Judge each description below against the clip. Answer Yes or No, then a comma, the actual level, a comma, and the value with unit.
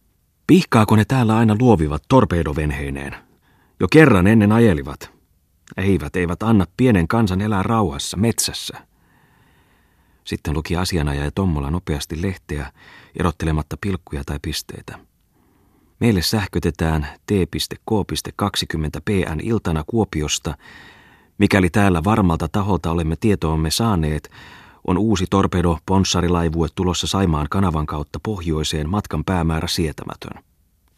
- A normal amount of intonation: Yes, average, 4.5 semitones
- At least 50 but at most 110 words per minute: Yes, average, 100 wpm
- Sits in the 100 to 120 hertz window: No, very low, 90 Hz